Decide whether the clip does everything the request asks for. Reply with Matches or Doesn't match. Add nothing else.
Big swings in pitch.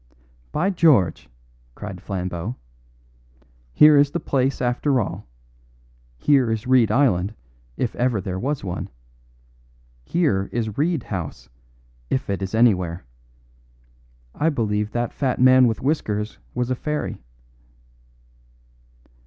Matches